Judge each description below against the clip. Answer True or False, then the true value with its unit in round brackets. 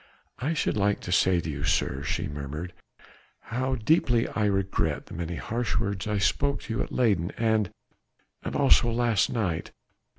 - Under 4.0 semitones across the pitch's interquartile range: False (5.2 semitones)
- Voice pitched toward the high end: False (105 Hz)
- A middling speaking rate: True (170 wpm)